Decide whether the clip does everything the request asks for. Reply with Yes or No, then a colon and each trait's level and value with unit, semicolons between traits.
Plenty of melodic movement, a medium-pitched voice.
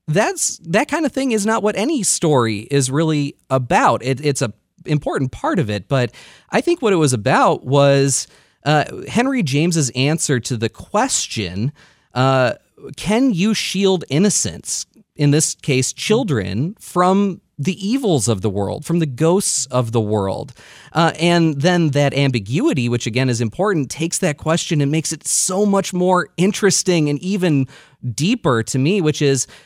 Yes: wide, 5.7 semitones; medium, 150 Hz